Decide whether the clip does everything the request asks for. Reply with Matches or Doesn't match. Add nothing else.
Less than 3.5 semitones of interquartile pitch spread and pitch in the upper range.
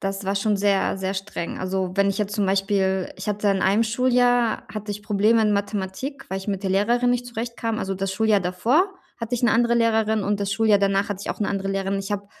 Matches